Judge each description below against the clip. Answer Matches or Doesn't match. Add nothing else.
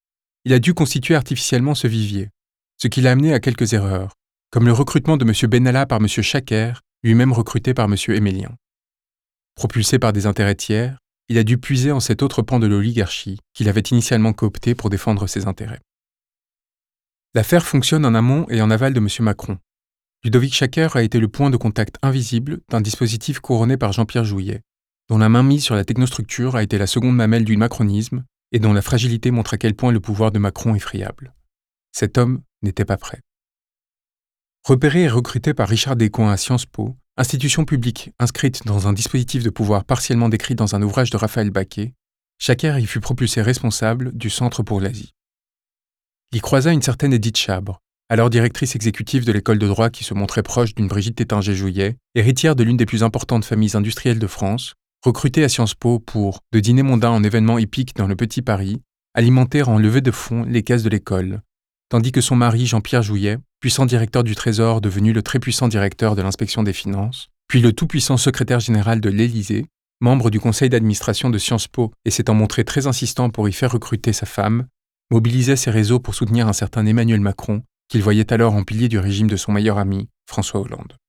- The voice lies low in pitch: Matches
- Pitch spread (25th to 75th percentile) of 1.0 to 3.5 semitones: Matches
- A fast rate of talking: Doesn't match